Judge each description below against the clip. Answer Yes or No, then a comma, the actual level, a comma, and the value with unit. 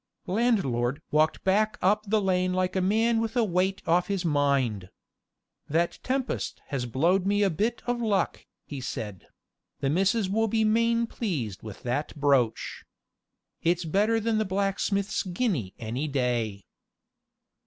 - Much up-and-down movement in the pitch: Yes, wide, 7.4 semitones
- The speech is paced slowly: No, average, 145 wpm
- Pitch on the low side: No, medium, 185 Hz